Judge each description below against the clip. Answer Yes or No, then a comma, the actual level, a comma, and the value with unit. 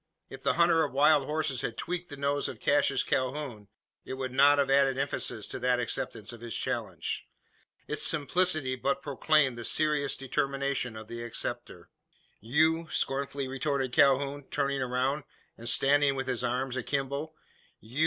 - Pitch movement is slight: Yes, narrow, 2.3 semitones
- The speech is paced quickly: No, average, 160 wpm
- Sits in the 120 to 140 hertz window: Yes, low, 135 Hz